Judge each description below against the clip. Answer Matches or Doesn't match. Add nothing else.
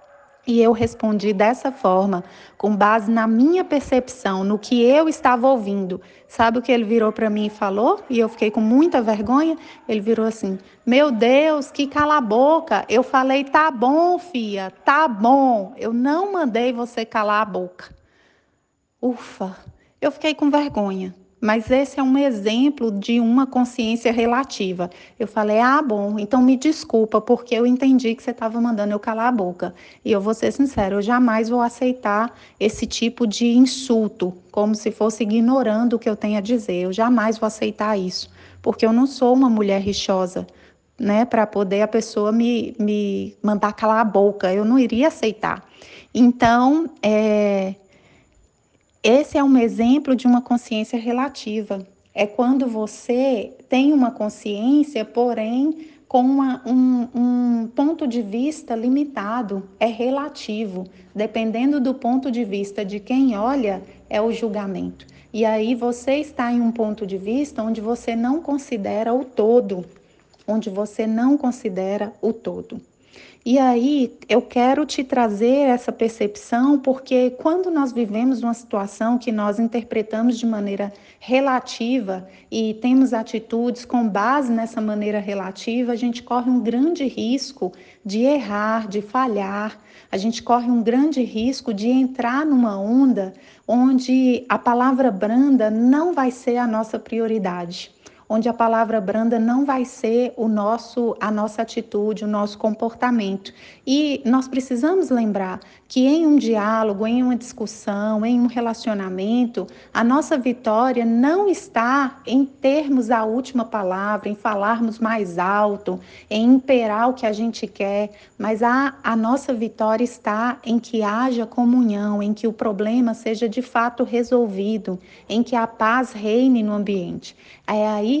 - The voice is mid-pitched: Doesn't match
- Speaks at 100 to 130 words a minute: Doesn't match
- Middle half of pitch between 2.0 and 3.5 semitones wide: Matches